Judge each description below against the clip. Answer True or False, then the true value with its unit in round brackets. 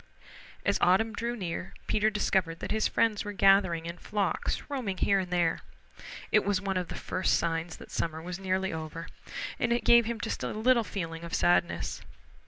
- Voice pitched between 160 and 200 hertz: True (190 Hz)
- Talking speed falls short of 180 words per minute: False (190 wpm)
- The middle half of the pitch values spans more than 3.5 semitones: True (4.1 semitones)